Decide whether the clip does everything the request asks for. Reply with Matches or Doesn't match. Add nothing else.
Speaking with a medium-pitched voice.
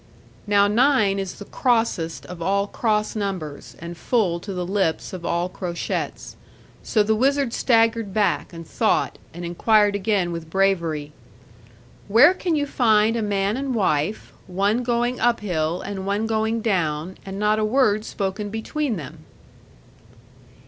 Doesn't match